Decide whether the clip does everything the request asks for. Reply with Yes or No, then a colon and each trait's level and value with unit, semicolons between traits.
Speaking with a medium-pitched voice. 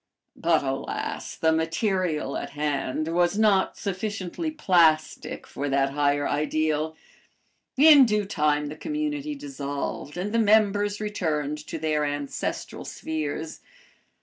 Yes: medium, 160 Hz